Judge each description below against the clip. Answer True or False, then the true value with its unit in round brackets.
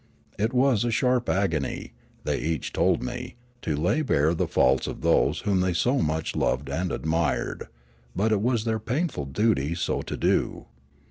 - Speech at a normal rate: True (175 wpm)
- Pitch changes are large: True (6.9 semitones)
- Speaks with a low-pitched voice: True (95 Hz)